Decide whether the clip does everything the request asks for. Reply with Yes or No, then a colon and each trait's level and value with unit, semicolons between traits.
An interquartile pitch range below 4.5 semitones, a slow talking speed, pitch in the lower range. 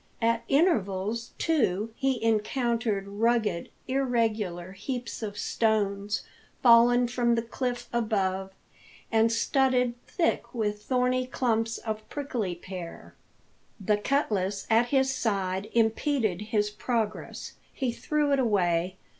No: average, 3.3 semitones; slow, 115 wpm; high, 225 Hz